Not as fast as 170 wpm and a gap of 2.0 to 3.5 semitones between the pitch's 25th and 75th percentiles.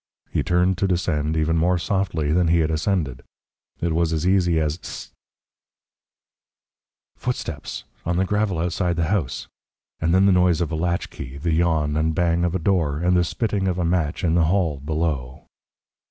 No: average, 180 wpm; narrow, 2.4 semitones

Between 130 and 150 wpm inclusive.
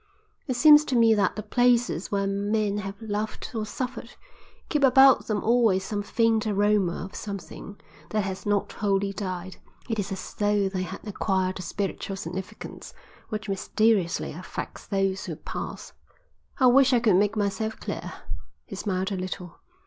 No: average, 165 wpm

